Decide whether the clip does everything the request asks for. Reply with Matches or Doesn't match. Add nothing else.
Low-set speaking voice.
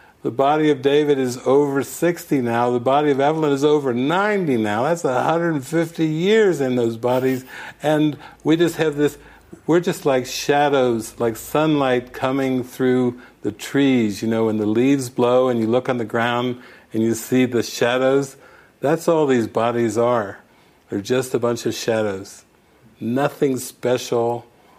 Matches